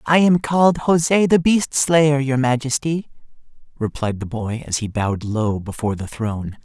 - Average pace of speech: Yes, average, 170 wpm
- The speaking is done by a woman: No, male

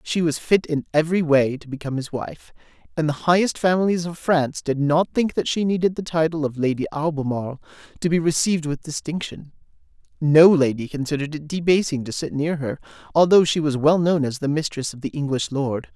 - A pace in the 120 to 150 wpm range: No, average, 200 wpm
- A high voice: No, medium, 155 Hz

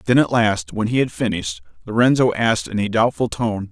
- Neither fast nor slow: No, fast, 210 wpm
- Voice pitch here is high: No, low, 110 Hz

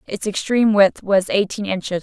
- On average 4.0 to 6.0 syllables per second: Yes, 5.2 syllables/s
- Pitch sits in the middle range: No, high, 200 Hz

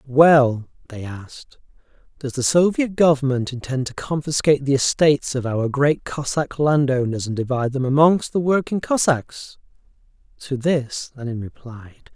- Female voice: No, male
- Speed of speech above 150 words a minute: No, average, 145 wpm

